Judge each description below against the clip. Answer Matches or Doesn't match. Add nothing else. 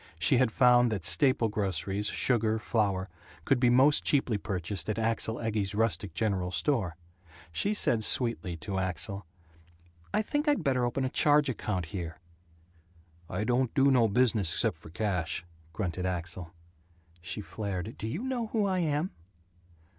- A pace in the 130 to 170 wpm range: Matches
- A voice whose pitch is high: Doesn't match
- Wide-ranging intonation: Matches